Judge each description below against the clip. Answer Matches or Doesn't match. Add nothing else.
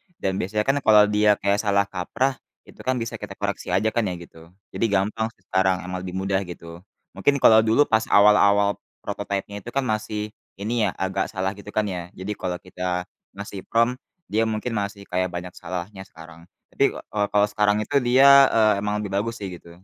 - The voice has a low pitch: Matches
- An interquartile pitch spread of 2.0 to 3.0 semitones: Matches